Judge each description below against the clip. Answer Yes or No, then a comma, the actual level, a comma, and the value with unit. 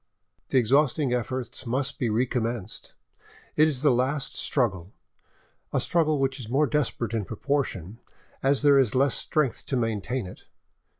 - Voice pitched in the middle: No, low, 130 Hz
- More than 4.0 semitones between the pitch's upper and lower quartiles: No, average, 3.5 semitones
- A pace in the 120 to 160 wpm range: Yes, average, 140 wpm